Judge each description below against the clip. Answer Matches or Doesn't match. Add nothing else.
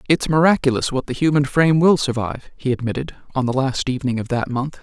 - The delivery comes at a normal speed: Doesn't match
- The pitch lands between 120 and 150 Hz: Matches